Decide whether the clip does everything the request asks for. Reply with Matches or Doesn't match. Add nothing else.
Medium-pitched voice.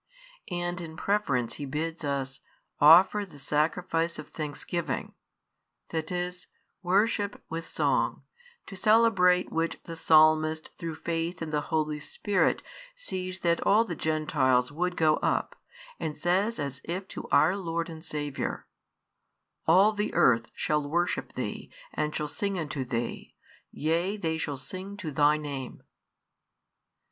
Matches